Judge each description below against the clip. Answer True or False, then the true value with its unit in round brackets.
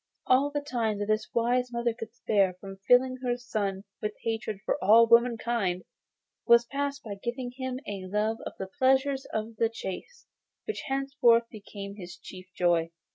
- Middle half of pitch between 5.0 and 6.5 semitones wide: False (3.9 semitones)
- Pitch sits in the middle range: False (230 Hz)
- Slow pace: False (170 wpm)